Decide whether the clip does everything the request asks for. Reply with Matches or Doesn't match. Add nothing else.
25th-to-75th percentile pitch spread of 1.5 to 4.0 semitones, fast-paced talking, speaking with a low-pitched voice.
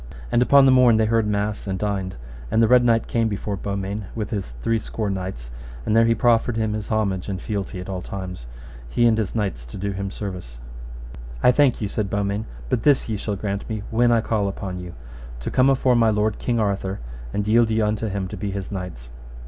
Matches